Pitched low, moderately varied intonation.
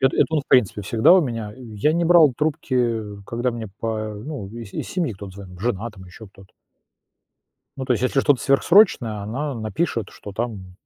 Yes: low, 115 Hz; average, 4.9 semitones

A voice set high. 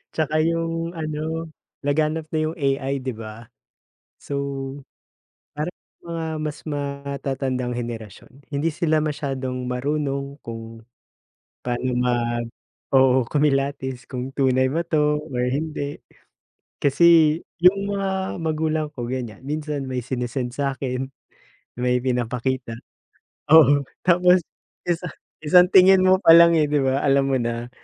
No: medium, 140 Hz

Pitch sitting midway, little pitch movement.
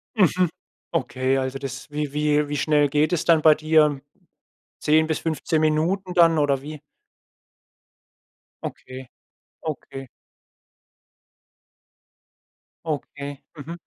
Yes: medium, 150 Hz; narrow, 2.1 semitones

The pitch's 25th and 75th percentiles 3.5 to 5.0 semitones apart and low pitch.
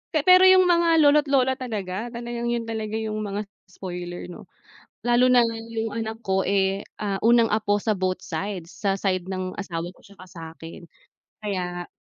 No: average, 4.2 semitones; high, 210 Hz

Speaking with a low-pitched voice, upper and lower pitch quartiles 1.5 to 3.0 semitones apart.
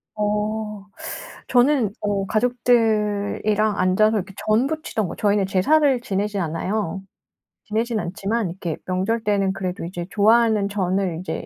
No: high, 210 Hz; narrow, 2.5 semitones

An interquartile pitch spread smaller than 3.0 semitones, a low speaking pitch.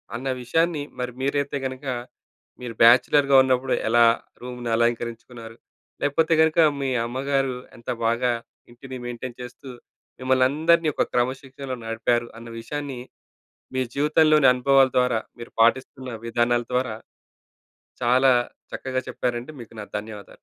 Yes: narrow, 2.5 semitones; low, 130 Hz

